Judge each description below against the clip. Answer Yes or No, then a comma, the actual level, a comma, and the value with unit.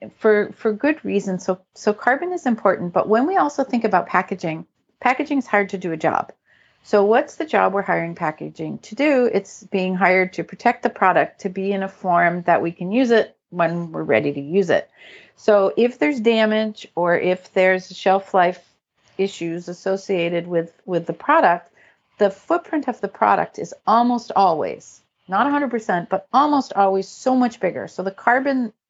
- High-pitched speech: Yes, high, 195 Hz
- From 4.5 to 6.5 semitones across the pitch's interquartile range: Yes, average, 4.9 semitones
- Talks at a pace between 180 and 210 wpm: Yes, average, 185 wpm